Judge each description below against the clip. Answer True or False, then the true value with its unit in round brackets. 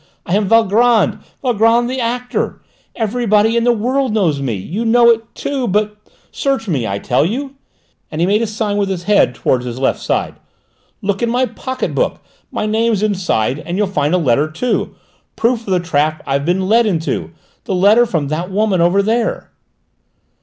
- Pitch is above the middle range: True (210 Hz)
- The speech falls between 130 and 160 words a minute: False (185 wpm)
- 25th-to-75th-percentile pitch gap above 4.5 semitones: True (5.3 semitones)